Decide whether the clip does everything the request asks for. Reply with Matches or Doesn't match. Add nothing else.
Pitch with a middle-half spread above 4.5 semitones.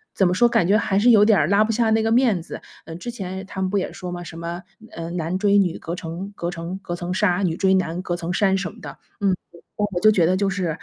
Doesn't match